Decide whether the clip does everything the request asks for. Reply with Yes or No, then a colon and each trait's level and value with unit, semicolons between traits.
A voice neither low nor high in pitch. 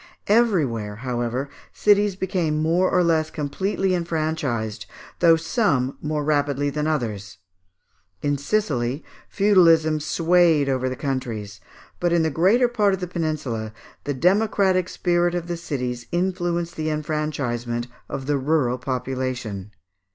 Yes: medium, 155 Hz